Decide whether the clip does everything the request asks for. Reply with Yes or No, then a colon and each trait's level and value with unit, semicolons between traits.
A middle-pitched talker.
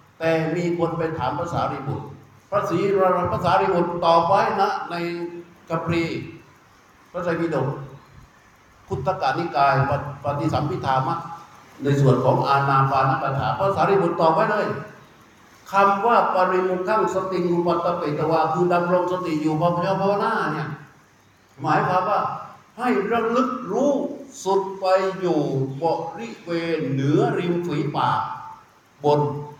Yes: medium, 170 Hz